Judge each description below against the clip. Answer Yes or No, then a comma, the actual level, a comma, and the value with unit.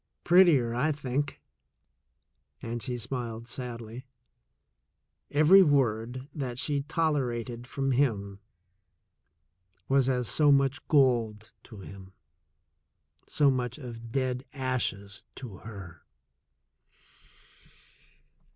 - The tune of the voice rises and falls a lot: No, average, 3.2 semitones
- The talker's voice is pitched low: Yes, low, 125 Hz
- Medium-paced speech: No, slow, 90 wpm